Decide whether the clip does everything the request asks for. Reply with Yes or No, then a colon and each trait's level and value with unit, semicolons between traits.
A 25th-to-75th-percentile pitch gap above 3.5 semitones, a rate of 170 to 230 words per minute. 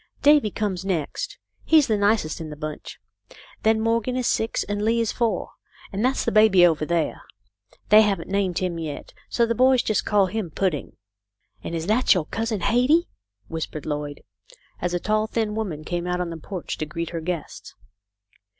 Yes: average, 4.9 semitones; average, 185 wpm